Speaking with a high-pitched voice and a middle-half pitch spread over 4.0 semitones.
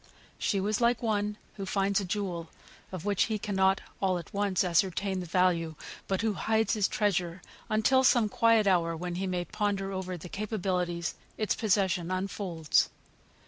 No: high, 195 Hz; average, 2.7 semitones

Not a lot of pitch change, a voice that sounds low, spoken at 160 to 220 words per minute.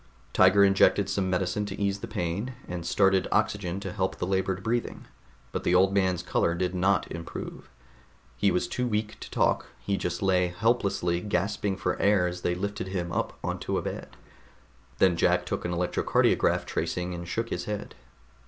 Yes: narrow, 2.3 semitones; very low, 95 Hz; average, 180 wpm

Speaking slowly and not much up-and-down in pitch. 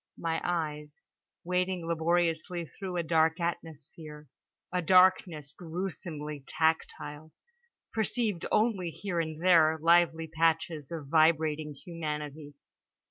Yes: slow, 100 wpm; narrow, 2.1 semitones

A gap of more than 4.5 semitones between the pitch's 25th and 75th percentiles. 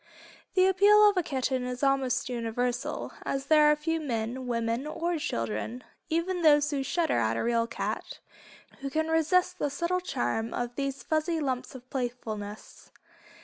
Yes: average, 5.2 semitones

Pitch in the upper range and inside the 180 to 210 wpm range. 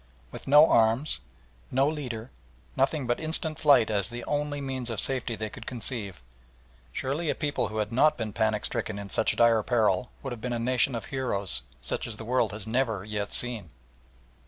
No: low, 120 Hz; average, 190 wpm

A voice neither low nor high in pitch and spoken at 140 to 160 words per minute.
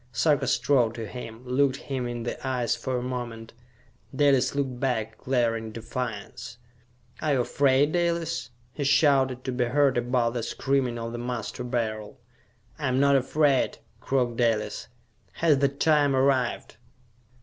No: low, 130 Hz; average, 150 wpm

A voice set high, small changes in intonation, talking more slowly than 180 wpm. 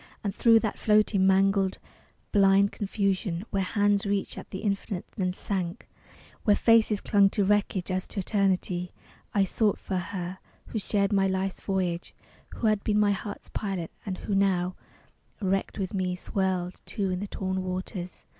Yes: high, 195 Hz; narrow, 1.6 semitones; average, 165 wpm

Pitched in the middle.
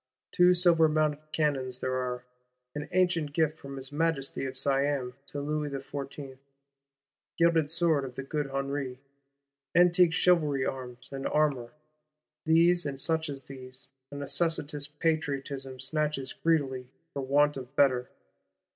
Yes: medium, 145 Hz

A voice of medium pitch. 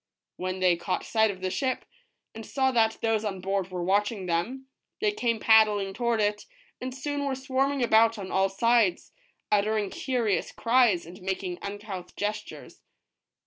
No: high, 210 Hz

